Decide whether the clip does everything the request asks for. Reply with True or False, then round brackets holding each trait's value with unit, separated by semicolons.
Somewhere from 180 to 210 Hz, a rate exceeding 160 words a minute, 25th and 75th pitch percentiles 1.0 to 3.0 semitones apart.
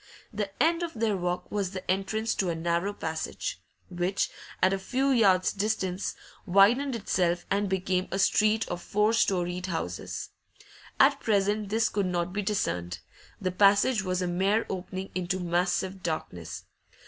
False (190 Hz; 155 wpm; 2.7 semitones)